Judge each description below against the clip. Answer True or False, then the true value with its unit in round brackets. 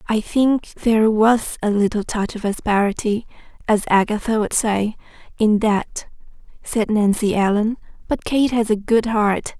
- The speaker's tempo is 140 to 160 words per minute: True (150 wpm)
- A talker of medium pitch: False (215 Hz)